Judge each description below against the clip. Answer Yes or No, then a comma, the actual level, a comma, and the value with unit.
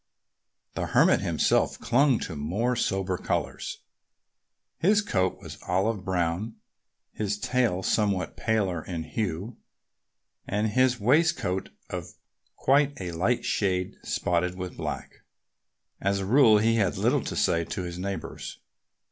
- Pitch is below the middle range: Yes, low, 100 Hz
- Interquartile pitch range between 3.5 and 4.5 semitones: Yes, average, 4.2 semitones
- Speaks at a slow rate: Yes, slow, 130 wpm